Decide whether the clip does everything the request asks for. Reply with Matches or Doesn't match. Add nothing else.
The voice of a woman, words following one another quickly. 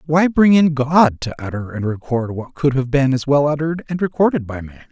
Doesn't match